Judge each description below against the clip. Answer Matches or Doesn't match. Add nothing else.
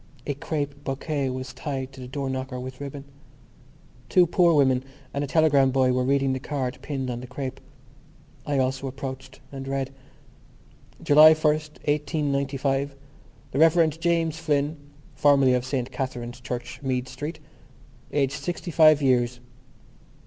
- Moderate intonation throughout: Doesn't match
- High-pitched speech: Doesn't match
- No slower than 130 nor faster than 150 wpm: Matches